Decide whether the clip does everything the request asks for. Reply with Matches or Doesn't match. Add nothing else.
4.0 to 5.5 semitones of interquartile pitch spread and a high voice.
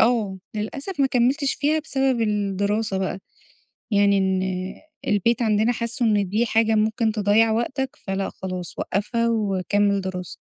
Doesn't match